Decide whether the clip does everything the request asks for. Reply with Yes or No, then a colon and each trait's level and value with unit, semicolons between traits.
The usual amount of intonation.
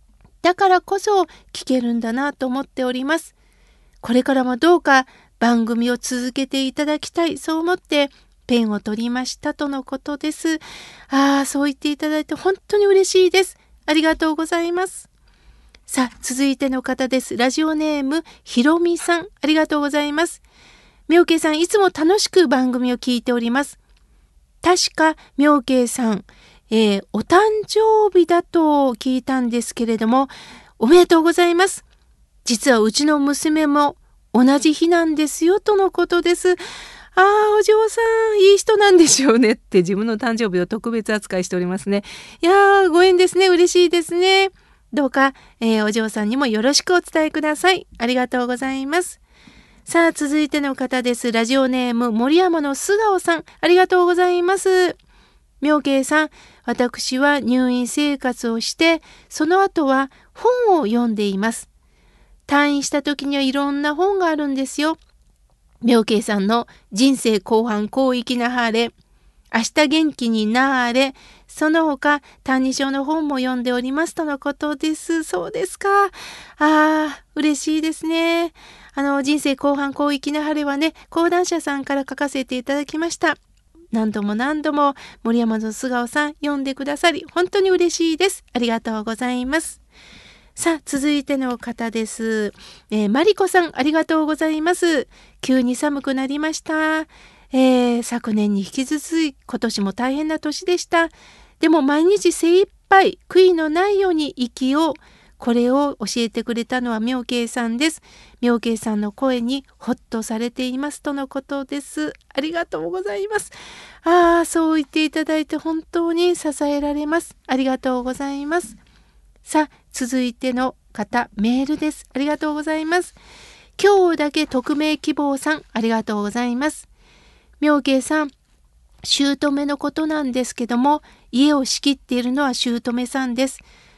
Yes: average, 4.7 semitones